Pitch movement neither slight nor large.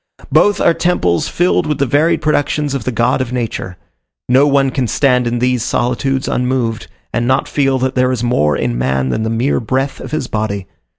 Yes: average, 3.2 semitones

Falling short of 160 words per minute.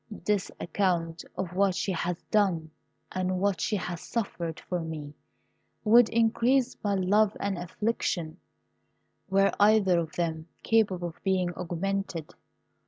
Yes: slow, 135 wpm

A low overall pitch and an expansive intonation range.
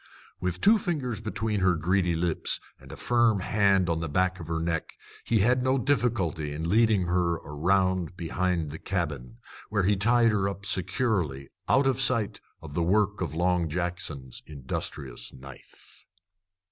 No: very low, 90 Hz; average, 4.7 semitones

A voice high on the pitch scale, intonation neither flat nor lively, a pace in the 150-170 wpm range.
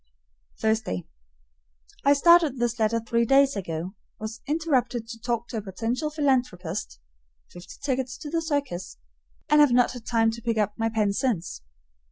Yes: high, 235 Hz; average, 4.0 semitones; average, 160 wpm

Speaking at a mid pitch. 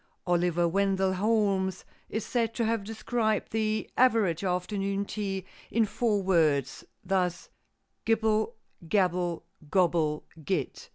No: high, 195 Hz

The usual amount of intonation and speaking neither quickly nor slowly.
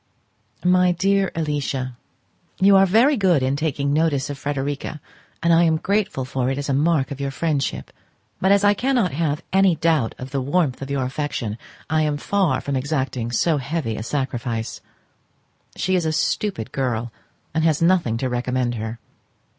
Yes: average, 4.7 semitones; average, 170 wpm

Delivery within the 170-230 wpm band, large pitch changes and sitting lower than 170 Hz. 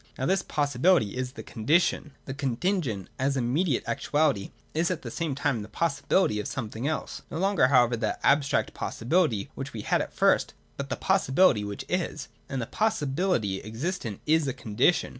Yes: average, 185 wpm; wide, 6.0 semitones; low, 135 Hz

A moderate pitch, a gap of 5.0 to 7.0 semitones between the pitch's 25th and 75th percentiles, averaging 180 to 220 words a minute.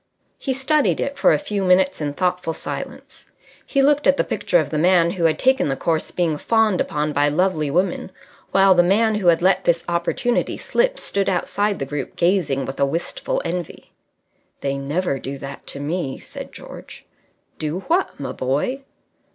Yes: medium, 175 Hz; average, 5.3 semitones; average, 185 wpm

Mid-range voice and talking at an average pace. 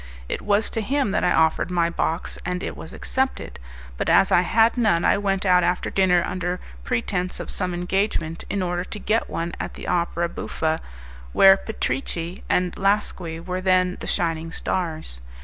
Yes: medium, 180 Hz; average, 180 wpm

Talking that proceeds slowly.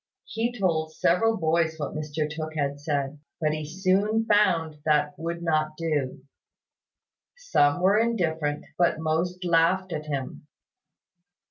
Yes: slow, 130 wpm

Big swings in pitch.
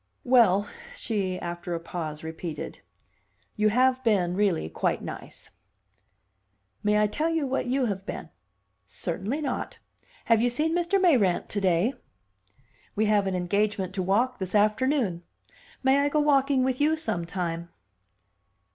Yes: wide, 6.2 semitones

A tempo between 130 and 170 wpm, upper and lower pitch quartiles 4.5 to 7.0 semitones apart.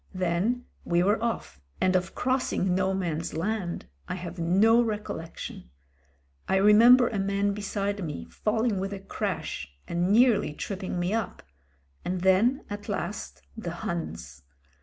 No: average, 160 wpm; average, 3.6 semitones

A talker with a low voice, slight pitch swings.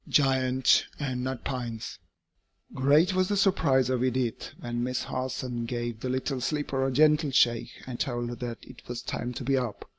Yes: low, 130 Hz; narrow, 2.1 semitones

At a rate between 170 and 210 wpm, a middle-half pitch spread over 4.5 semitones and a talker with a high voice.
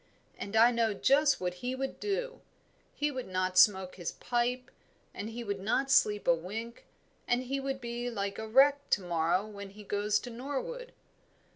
Yes: average, 180 wpm; average, 5.0 semitones; high, 230 Hz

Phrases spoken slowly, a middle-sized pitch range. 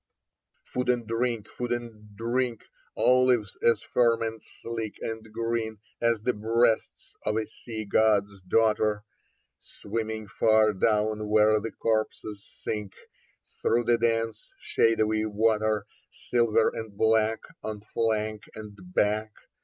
No: slow, 120 wpm; narrow, 1.3 semitones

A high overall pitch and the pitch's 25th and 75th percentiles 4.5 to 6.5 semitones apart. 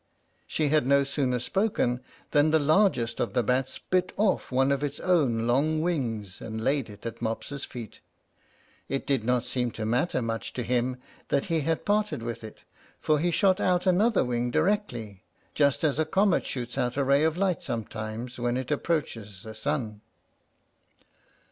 No: low, 135 Hz; average, 5.0 semitones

